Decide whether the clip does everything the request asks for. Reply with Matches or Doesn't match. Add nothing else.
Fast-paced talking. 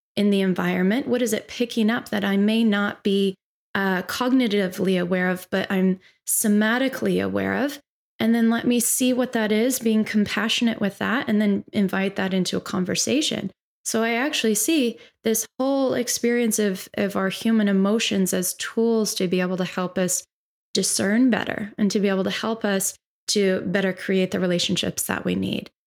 Doesn't match